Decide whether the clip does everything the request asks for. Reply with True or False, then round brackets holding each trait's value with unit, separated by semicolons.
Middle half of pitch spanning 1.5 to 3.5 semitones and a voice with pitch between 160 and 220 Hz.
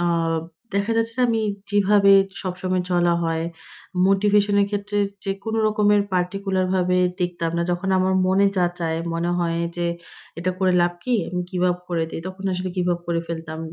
True (2.4 semitones; 185 Hz)